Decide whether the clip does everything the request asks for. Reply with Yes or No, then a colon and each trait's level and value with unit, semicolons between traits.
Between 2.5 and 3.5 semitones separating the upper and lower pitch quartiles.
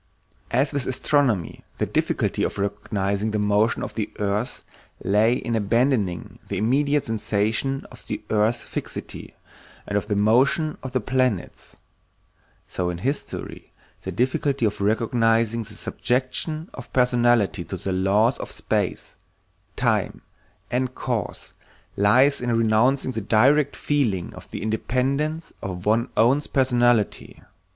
No: average, 4.0 semitones